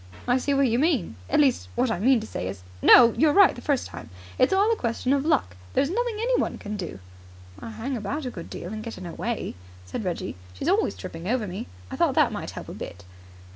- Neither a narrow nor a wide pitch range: No, wide, 7.6 semitones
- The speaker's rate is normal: No, fast, 250 wpm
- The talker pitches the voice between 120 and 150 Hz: No, high, 235 Hz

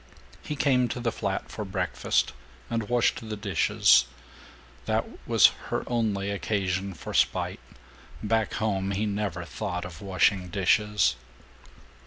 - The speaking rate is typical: No, slow, 130 wpm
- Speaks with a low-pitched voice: Yes, low, 100 Hz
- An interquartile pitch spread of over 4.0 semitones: No, average, 2.7 semitones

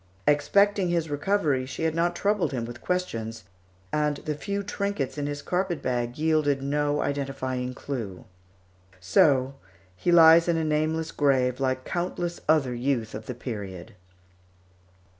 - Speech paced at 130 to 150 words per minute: Yes, average, 140 wpm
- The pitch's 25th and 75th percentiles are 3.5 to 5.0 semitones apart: Yes, average, 4.6 semitones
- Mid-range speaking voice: Yes, medium, 145 Hz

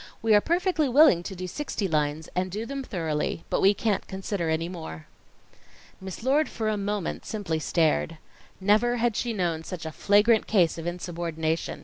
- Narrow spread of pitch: No, average, 5.1 semitones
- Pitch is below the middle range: No, high, 190 Hz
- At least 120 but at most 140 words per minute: No, average, 175 wpm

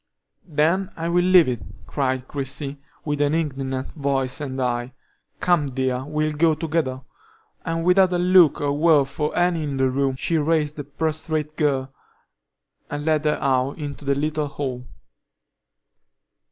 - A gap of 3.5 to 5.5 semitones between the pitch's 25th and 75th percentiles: No, average, 3.0 semitones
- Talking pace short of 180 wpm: Yes, average, 155 wpm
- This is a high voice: No, medium, 145 Hz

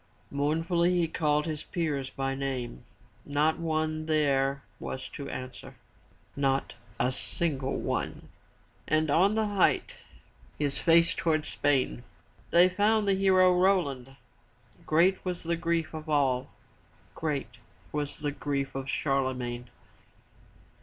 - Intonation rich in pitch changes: No, average, 3.7 semitones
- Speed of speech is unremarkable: No, slow, 125 wpm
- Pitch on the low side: No, medium, 150 Hz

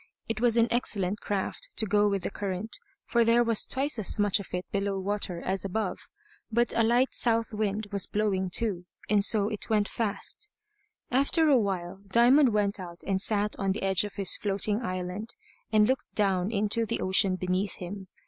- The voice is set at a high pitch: Yes, high, 205 Hz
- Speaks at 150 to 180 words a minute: No, average, 195 wpm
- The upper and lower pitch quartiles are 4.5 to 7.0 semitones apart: No, average, 2.8 semitones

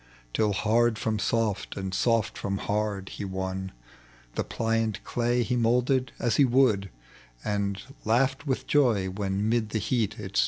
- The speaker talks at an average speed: Yes, average, 160 wpm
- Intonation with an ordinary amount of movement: Yes, average, 3.2 semitones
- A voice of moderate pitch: No, low, 110 Hz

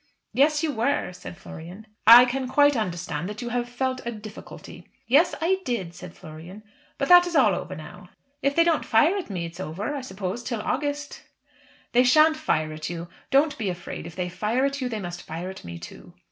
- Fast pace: Yes, fast, 215 wpm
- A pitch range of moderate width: No, wide, 7.8 semitones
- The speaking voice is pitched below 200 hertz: No, high, 230 Hz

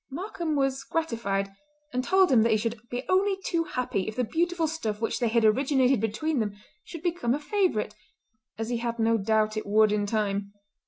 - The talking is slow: No, average, 200 wpm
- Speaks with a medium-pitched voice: No, high, 235 Hz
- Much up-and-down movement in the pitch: Yes, wide, 6.6 semitones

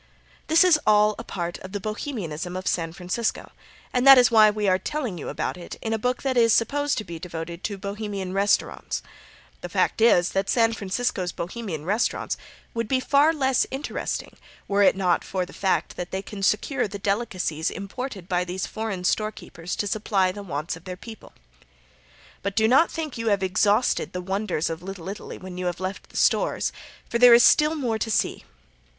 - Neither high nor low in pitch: No, high, 200 Hz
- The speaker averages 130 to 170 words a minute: No, average, 200 wpm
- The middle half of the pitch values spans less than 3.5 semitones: No, average, 4.2 semitones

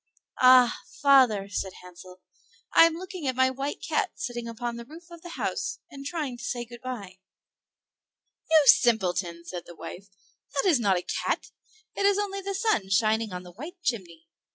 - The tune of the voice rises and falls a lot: Yes, wide, 8.2 semitones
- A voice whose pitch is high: Yes, high, 245 Hz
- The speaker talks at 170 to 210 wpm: Yes, average, 180 wpm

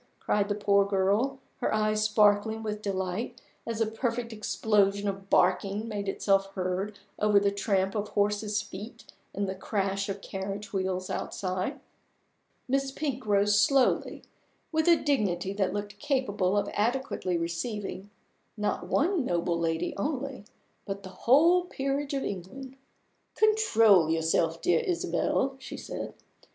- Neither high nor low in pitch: No, high, 205 Hz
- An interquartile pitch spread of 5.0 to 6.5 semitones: No, average, 4.1 semitones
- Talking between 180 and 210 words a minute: No, average, 140 wpm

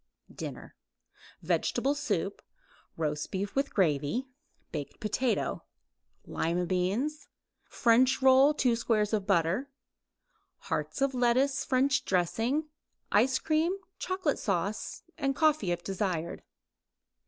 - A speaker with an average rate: No, slow, 95 wpm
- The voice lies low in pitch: No, high, 235 Hz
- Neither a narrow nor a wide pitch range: No, wide, 6.8 semitones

